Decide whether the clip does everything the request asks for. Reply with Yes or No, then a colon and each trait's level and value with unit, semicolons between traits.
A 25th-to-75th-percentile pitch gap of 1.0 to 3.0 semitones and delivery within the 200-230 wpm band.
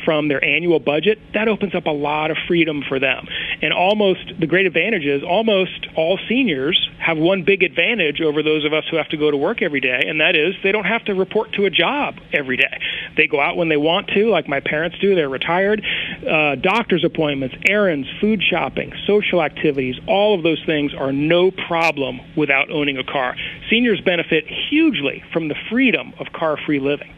No: average, 4.7 semitones; fast, 205 wpm